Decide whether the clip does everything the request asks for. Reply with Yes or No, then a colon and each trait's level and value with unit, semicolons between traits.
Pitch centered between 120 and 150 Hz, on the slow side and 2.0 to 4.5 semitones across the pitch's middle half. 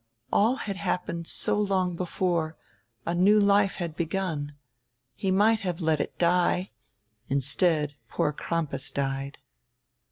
No: medium, 175 Hz; slow, 130 wpm; average, 3.9 semitones